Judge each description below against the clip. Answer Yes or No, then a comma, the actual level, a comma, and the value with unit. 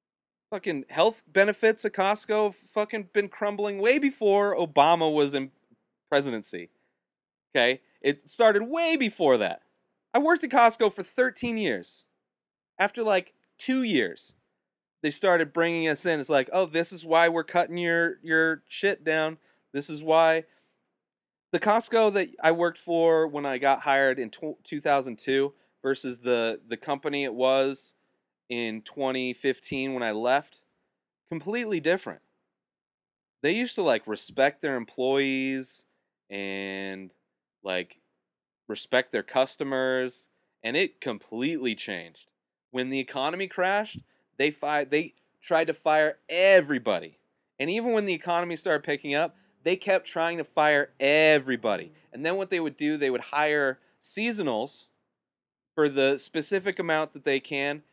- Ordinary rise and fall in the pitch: No, wide, 6.0 semitones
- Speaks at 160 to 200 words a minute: No, average, 140 wpm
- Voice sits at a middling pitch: Yes, medium, 155 Hz